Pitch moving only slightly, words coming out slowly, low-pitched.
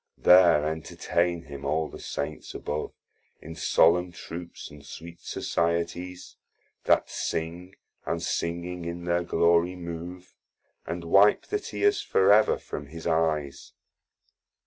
Yes: narrow, 1.5 semitones; slow, 125 wpm; very low, 85 Hz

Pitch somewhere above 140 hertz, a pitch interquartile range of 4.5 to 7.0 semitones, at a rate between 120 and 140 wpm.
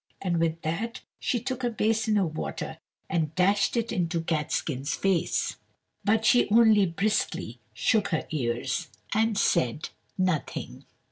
Yes: medium, 185 Hz; wide, 5.4 semitones; slow, 135 wpm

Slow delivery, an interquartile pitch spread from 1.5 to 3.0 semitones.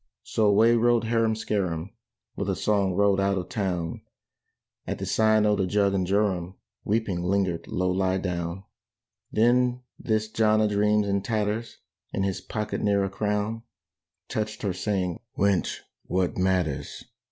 No: average, 150 wpm; narrow, 2.5 semitones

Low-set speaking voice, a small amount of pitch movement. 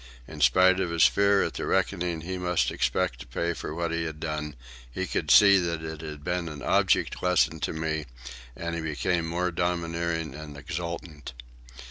Yes: very low, 85 Hz; narrow, 2.2 semitones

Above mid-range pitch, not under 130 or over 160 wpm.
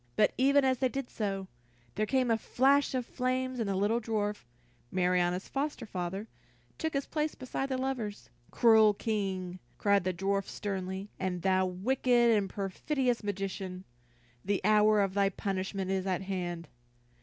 Yes: high, 205 Hz; average, 155 wpm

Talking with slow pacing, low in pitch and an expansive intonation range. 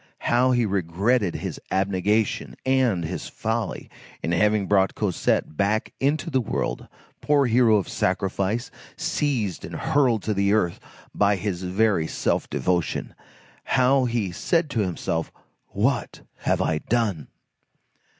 No: slow, 130 wpm; low, 105 Hz; average, 4.5 semitones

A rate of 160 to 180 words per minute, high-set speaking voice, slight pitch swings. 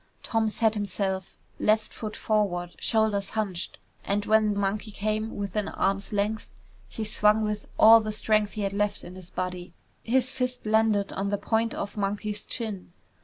Yes: average, 165 wpm; high, 210 Hz; narrow, 1.7 semitones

